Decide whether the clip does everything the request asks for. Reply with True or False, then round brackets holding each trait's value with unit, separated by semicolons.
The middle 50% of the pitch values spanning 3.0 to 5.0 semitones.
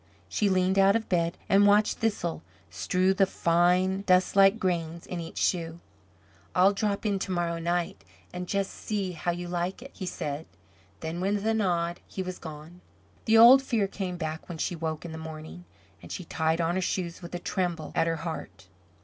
False (2.6 semitones)